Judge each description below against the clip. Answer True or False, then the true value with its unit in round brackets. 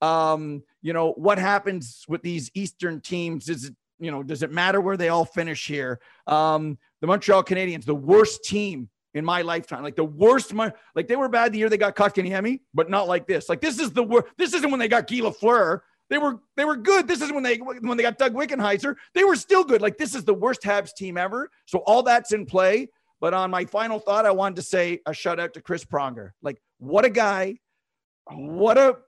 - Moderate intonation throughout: False (6.5 semitones)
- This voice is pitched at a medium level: False (195 Hz)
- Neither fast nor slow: False (230 wpm)